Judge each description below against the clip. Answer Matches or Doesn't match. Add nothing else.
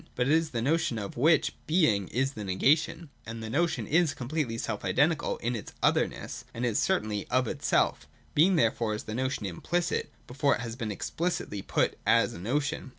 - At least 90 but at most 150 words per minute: Doesn't match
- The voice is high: Doesn't match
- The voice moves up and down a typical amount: Doesn't match